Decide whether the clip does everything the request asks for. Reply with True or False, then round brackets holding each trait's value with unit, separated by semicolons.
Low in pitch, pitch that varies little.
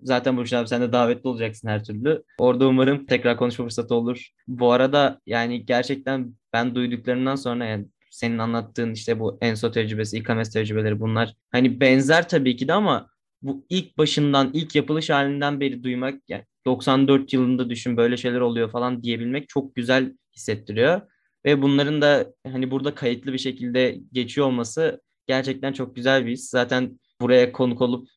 True (125 Hz; 2.2 semitones)